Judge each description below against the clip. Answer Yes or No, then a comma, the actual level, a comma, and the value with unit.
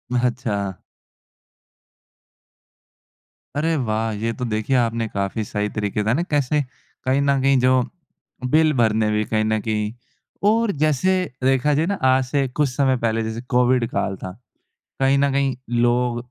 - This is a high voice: No, low, 125 Hz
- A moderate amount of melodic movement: Yes, average, 3.9 semitones